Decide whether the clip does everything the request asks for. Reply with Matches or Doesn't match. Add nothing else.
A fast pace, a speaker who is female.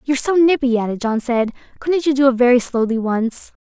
Matches